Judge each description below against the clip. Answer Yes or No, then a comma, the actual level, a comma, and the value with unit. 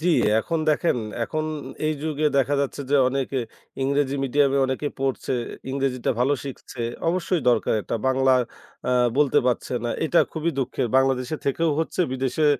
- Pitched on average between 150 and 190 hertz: No, low, 135 Hz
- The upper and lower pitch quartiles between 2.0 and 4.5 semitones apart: Yes, average, 2.7 semitones